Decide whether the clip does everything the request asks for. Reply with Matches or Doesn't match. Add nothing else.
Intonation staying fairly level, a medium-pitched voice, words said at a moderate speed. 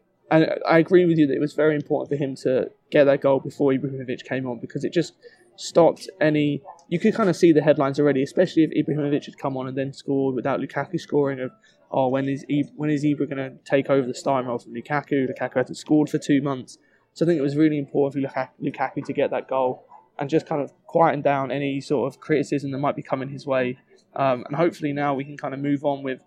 Doesn't match